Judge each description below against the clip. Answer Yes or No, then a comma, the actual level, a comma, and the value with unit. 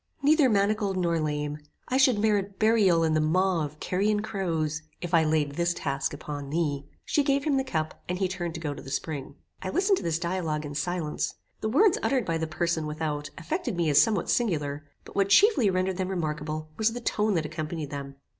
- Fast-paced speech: Yes, fast, 210 wpm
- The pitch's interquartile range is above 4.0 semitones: Yes, average, 5.3 semitones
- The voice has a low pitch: No, medium, 170 Hz